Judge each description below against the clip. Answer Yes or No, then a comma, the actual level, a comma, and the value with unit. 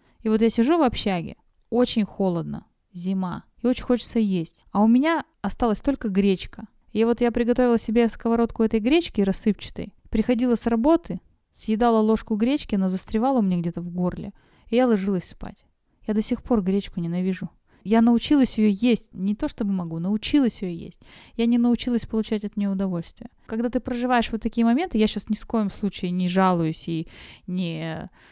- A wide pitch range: No, average, 3.8 semitones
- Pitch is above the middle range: Yes, high, 220 Hz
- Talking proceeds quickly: Yes, fast, 180 wpm